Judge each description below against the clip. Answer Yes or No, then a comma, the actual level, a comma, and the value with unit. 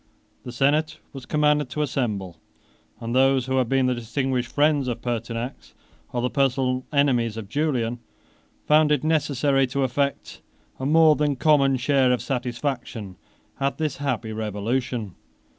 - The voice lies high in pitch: No, low, 130 Hz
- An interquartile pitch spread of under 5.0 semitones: Yes, average, 3.0 semitones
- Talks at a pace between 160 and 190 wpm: No, average, 145 wpm